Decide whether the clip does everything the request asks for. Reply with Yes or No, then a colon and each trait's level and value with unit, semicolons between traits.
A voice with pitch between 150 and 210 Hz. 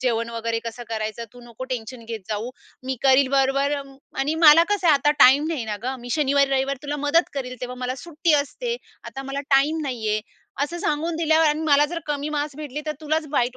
No: very high, 275 Hz